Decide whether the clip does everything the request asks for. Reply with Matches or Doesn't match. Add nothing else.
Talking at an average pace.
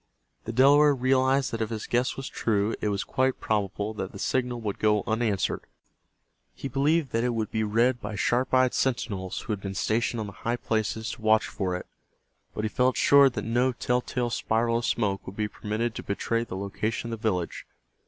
Doesn't match